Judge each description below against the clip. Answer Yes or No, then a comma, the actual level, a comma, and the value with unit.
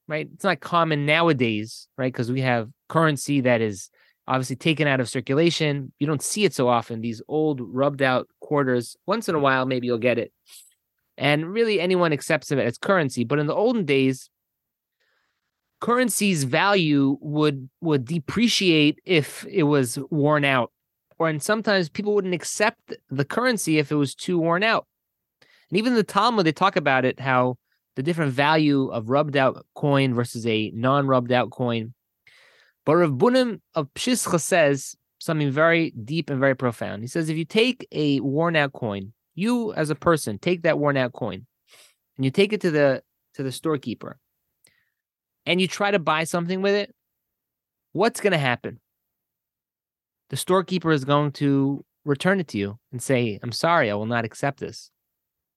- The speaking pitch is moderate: Yes, medium, 145 Hz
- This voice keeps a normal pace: Yes, average, 170 wpm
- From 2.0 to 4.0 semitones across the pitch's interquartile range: No, average, 4.8 semitones